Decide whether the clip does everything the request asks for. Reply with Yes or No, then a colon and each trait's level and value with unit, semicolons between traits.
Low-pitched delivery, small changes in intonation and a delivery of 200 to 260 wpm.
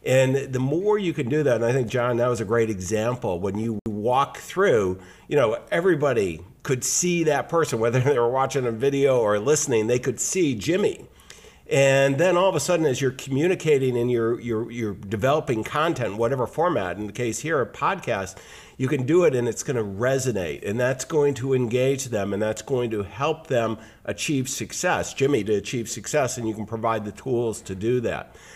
No: low, 125 Hz; average, 3.6 semitones; fast, 205 wpm